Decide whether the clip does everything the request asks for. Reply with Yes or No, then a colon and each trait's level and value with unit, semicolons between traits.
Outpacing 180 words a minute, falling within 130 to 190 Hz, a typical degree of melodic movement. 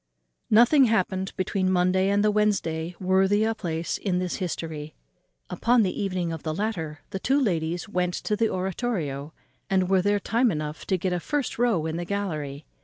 Yes: average, 190 wpm; medium, 185 Hz; average, 4.2 semitones